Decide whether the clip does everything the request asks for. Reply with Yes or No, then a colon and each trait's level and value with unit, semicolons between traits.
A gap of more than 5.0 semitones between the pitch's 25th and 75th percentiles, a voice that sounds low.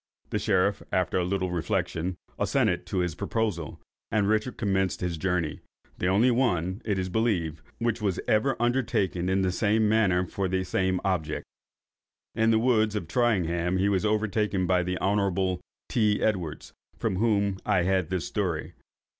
No: average, 3.1 semitones; very low, 95 Hz